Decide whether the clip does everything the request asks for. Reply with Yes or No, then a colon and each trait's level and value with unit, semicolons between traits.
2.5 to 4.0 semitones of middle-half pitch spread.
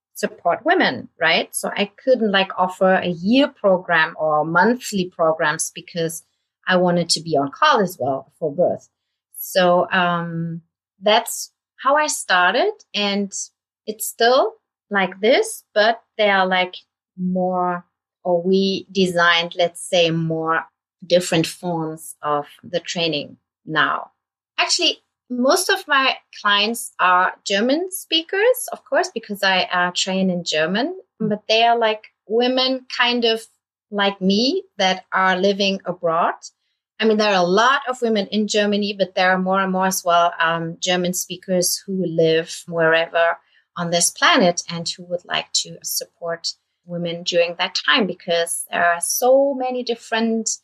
No: average, 4.7 semitones